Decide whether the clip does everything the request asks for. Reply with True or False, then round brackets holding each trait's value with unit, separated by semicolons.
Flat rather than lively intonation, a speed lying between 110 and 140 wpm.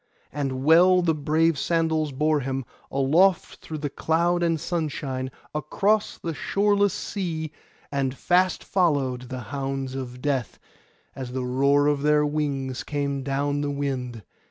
False (3.4 semitones; 135 wpm)